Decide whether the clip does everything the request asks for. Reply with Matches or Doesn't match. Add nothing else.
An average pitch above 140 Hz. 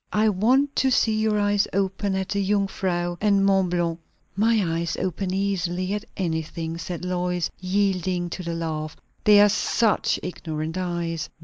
Matches